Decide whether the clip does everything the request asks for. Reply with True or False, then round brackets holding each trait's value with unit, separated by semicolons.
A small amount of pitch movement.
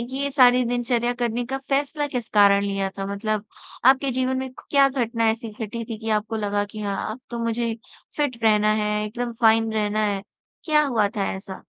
False (3.3 semitones)